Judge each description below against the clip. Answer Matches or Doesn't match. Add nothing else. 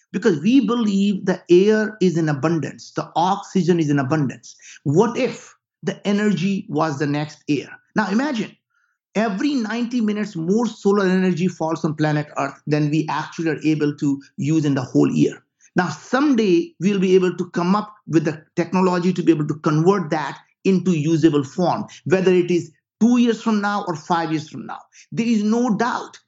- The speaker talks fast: Doesn't match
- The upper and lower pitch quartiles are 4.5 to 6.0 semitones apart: Matches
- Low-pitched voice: Doesn't match